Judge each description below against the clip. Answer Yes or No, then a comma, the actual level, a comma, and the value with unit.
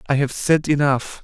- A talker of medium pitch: Yes, medium, 145 Hz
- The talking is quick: No, average, 195 wpm